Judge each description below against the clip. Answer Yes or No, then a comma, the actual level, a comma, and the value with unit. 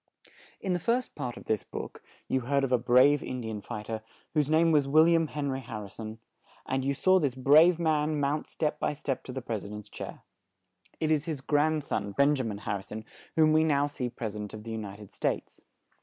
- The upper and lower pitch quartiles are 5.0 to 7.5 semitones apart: Yes, wide, 5.5 semitones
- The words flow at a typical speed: No, fast, 250 wpm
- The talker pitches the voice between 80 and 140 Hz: Yes, low, 135 Hz